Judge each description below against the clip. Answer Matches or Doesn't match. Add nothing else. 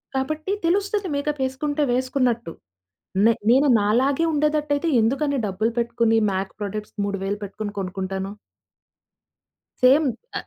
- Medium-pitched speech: Doesn't match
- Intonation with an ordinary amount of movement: Doesn't match